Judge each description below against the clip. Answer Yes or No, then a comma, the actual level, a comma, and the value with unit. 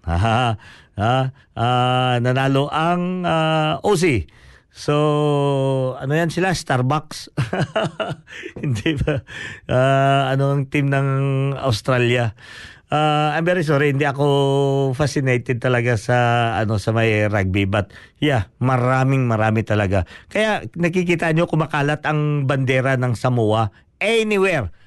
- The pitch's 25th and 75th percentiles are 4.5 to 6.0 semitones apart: No, average, 3.9 semitones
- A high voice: No, low, 135 Hz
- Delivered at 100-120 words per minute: Yes, average, 115 wpm